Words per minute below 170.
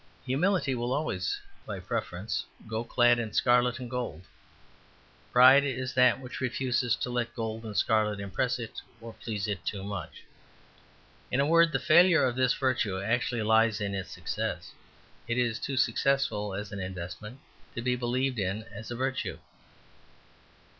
Yes: average, 160 wpm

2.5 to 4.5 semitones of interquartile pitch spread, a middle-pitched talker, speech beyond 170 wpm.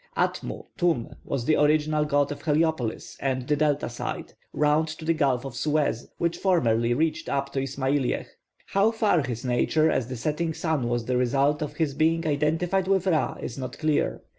Yes: average, 3.4 semitones; medium, 150 Hz; average, 185 wpm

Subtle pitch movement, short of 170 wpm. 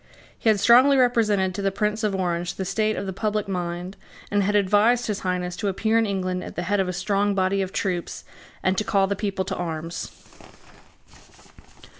No: narrow, 2.3 semitones; average, 200 wpm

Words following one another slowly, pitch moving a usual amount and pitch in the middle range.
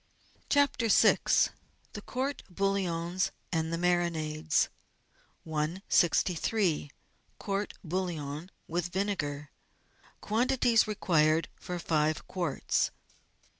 Yes: slow, 80 wpm; average, 4.0 semitones; medium, 175 Hz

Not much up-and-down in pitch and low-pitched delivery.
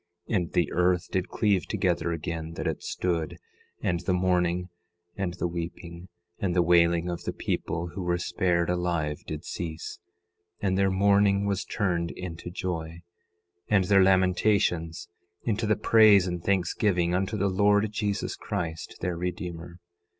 Yes: narrow, 2.3 semitones; very low, 90 Hz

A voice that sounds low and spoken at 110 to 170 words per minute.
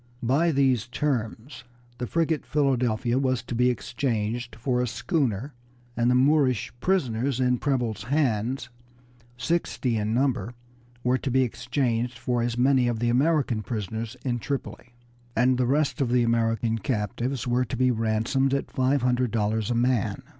Yes: low, 125 Hz; average, 155 wpm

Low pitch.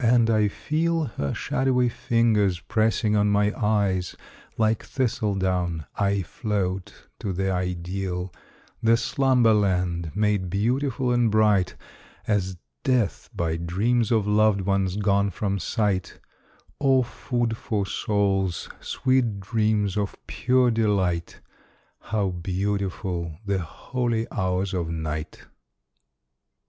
Yes: low, 100 Hz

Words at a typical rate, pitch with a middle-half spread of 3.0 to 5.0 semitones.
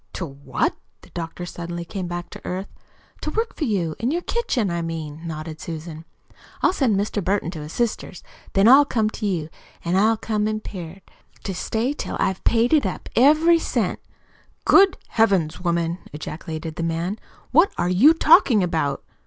No: average, 175 wpm; wide, 5.4 semitones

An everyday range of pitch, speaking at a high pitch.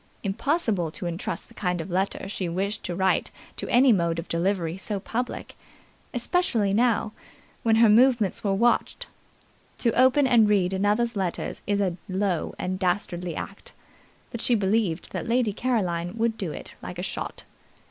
Yes: average, 4.3 semitones; high, 200 Hz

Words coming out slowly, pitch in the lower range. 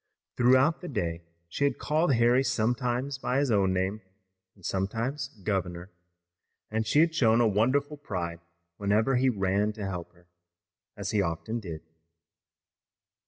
No: average, 145 wpm; low, 110 Hz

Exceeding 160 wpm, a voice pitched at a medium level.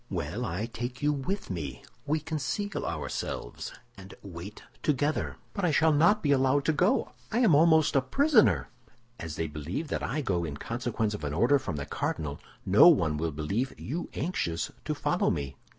No: average, 180 wpm; low, 125 Hz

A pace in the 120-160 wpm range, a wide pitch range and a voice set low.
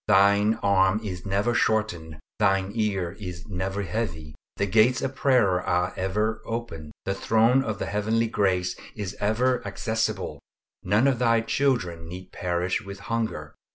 No: average, 150 wpm; average, 3.5 semitones; low, 100 Hz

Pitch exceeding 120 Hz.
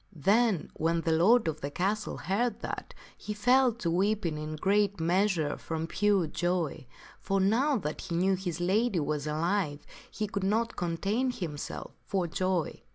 Yes: medium, 185 Hz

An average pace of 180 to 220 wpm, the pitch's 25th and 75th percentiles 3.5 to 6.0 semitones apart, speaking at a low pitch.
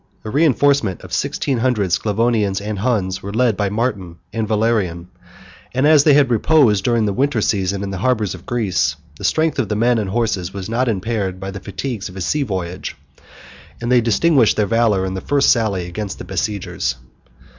Yes: average, 190 wpm; average, 4.0 semitones; low, 105 Hz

